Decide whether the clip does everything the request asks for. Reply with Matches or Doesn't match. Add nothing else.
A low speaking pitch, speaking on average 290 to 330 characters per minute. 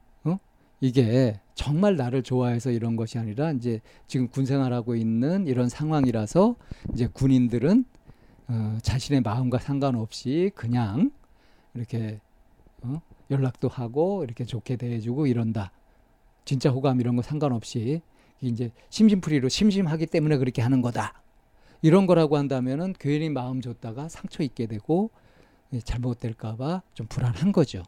Matches